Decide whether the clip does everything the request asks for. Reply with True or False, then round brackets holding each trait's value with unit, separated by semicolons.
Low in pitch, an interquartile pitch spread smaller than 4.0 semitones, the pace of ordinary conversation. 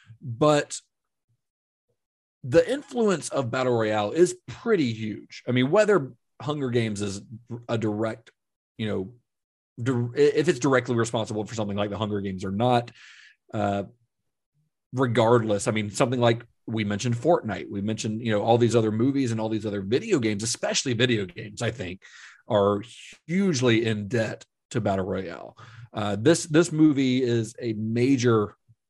True (115 Hz; 3.4 semitones; 155 wpm)